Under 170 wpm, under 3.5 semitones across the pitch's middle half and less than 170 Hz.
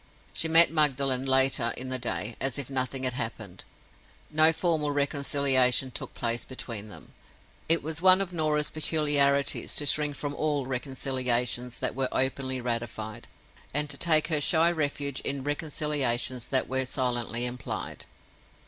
Yes: average, 150 wpm; average, 3.1 semitones; low, 135 Hz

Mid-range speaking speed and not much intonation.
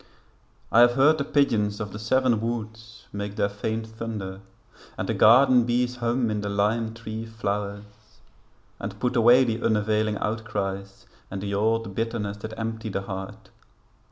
Yes: average, 155 wpm; narrow, 2.2 semitones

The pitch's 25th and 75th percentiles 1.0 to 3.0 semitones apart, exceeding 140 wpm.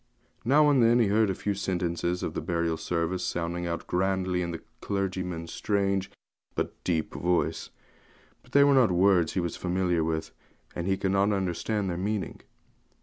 Yes: narrow, 2.5 semitones; average, 170 wpm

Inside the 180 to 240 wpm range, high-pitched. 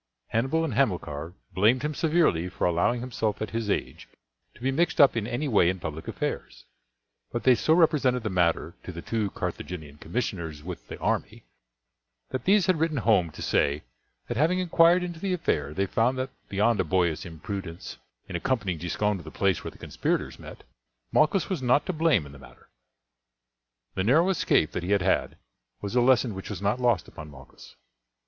No: average, 190 wpm; low, 110 Hz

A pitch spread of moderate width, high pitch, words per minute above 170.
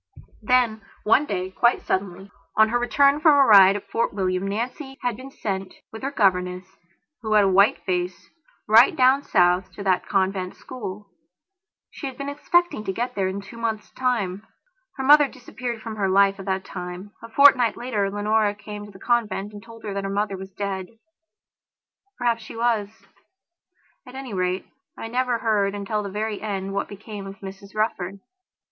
Yes: average, 3.6 semitones; high, 210 Hz; average, 180 wpm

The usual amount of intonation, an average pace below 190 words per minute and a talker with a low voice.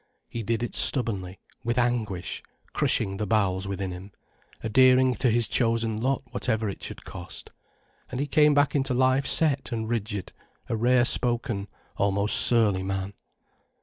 Yes: average, 4.2 semitones; average, 150 wpm; low, 115 Hz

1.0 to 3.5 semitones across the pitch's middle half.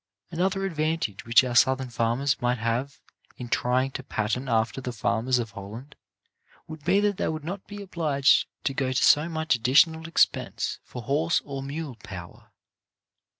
No: average, 4.9 semitones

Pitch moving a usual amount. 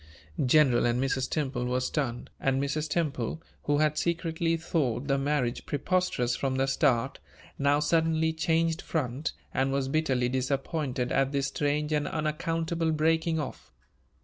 Yes: average, 3.3 semitones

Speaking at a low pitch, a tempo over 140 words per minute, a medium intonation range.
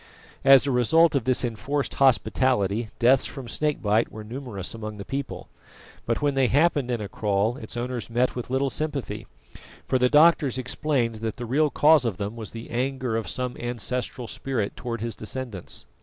Yes: low, 125 Hz; average, 185 wpm; average, 3.2 semitones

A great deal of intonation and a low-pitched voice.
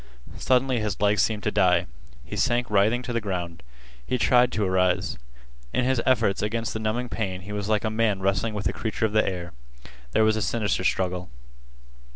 No: average, 3.2 semitones; low, 105 Hz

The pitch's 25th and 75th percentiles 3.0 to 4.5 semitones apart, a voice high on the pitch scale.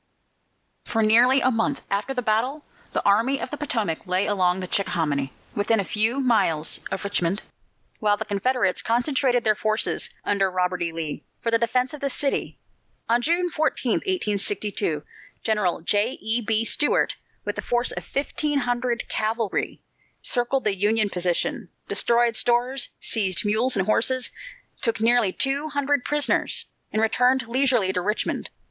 Yes: average, 4.2 semitones; high, 225 Hz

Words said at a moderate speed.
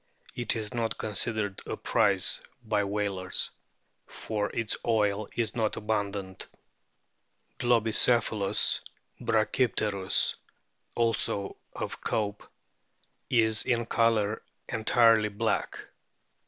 No: slow, 85 wpm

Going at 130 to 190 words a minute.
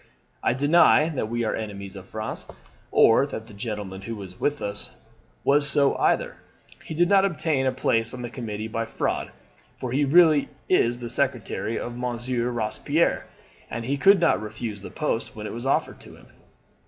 Yes: average, 185 wpm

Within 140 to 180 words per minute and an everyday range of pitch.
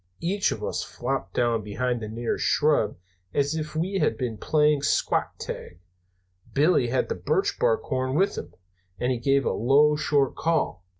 Yes: average, 175 wpm; average, 4.3 semitones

